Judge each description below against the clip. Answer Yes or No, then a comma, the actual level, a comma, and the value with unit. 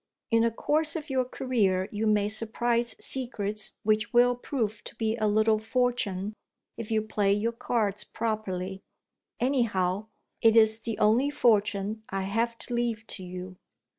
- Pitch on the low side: No, high, 220 Hz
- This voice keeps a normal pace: Yes, average, 155 wpm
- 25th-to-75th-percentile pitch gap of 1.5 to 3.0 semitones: Yes, narrow, 2.5 semitones